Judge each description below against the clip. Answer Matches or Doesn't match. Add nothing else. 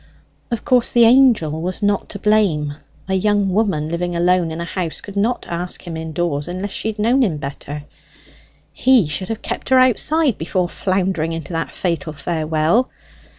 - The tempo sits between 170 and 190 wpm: Matches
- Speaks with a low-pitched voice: Doesn't match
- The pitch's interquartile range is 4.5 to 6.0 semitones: Matches